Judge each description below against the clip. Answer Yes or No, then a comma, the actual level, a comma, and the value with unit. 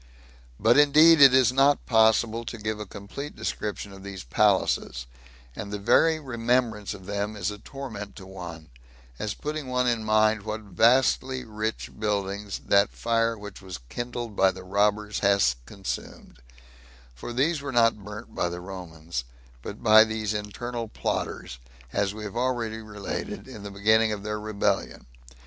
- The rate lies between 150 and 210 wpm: Yes, average, 160 wpm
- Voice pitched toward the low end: Yes, low, 110 Hz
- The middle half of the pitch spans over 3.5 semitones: No, average, 2.9 semitones